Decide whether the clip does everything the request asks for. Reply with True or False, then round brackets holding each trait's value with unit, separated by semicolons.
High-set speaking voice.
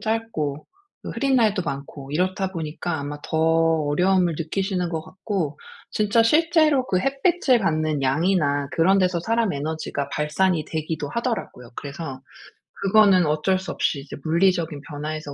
False (170 Hz)